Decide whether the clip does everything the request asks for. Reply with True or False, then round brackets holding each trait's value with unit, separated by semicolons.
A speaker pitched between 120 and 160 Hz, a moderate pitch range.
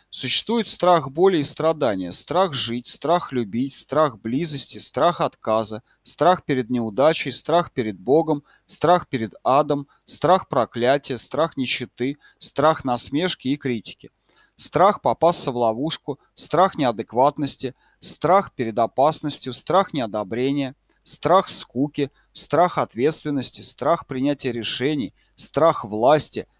True (140 Hz; 4.6 semitones)